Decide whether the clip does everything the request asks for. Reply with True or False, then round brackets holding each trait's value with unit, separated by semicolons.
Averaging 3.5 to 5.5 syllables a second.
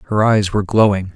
False (6.5 syllables/s)